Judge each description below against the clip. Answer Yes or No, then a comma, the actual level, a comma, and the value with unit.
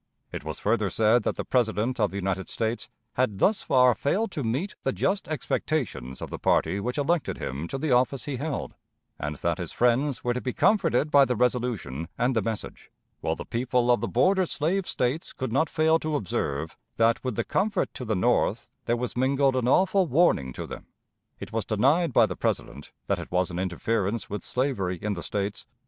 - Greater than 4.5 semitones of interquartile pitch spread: Yes, wide, 5.5 semitones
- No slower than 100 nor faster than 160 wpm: No, fast, 205 wpm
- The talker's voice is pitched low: Yes, low, 125 Hz